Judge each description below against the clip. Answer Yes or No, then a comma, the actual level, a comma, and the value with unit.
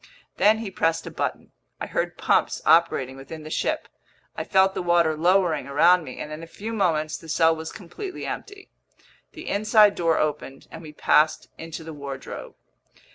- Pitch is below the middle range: No, medium, 165 Hz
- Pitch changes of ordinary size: Yes, average, 3.8 semitones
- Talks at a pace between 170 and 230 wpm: Yes, average, 180 wpm